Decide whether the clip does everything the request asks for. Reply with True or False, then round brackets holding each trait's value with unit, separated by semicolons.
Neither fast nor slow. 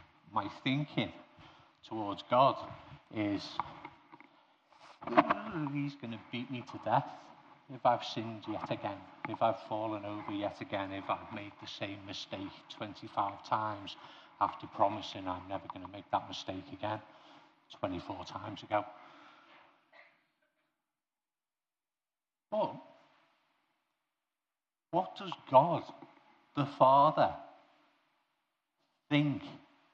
False (105 wpm)